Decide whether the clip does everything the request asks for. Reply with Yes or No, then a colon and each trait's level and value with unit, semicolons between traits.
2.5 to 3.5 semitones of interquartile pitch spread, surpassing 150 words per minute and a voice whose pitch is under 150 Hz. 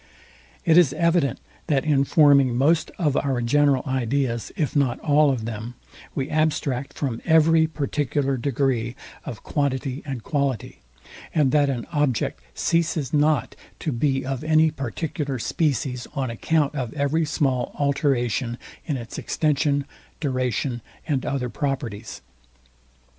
No: average, 3.0 semitones; slow, 135 wpm; medium, 140 Hz